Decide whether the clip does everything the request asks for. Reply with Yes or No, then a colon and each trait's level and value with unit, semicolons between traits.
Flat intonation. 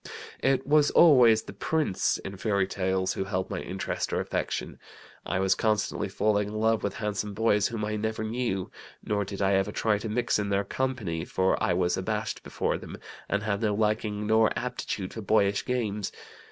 Yes: narrow, 2.3 semitones